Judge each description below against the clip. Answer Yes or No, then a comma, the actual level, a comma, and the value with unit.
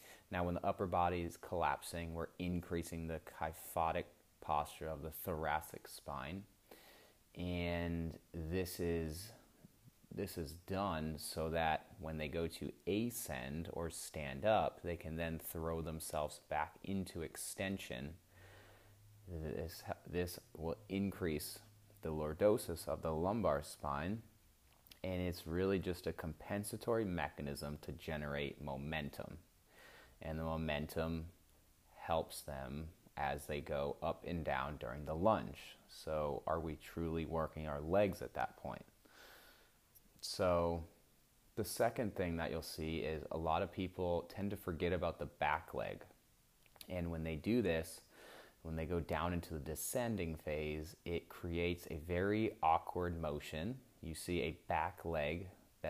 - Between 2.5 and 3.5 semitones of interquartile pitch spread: Yes, average, 2.9 semitones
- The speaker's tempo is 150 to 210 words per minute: No, slow, 135 wpm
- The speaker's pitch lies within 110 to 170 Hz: No, very low, 85 Hz